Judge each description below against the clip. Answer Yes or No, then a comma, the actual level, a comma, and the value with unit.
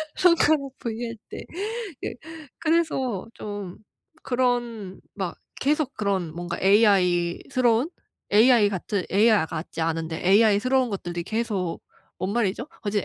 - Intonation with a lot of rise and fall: No, average, 4.8 semitones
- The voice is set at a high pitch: Yes, high, 210 Hz